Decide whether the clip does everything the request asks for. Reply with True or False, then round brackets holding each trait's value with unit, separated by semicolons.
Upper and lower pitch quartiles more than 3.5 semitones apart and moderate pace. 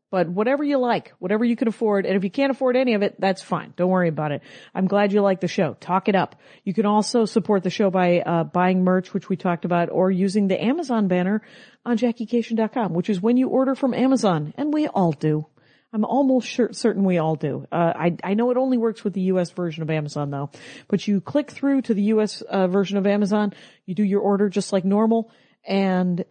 False (3.9 semitones; 235 wpm)